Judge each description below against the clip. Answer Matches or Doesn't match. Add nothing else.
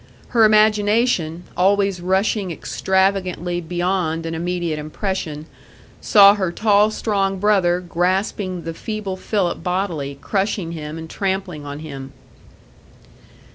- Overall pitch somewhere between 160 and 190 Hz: Matches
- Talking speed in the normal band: Doesn't match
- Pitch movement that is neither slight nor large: Matches